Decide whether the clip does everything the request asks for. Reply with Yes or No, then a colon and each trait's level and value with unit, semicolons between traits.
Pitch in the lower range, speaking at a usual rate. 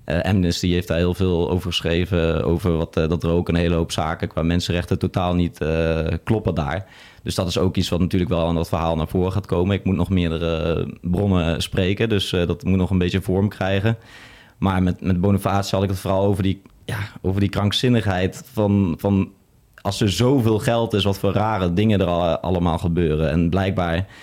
No: very low, 95 Hz; fast, 210 wpm